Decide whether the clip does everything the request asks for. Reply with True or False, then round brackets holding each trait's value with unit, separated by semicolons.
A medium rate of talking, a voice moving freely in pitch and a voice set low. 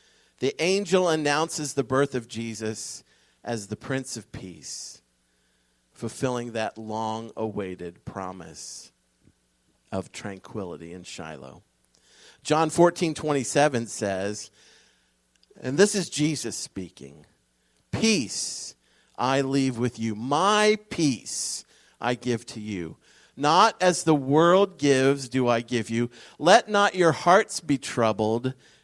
False (115 wpm; 6.9 semitones; 120 Hz)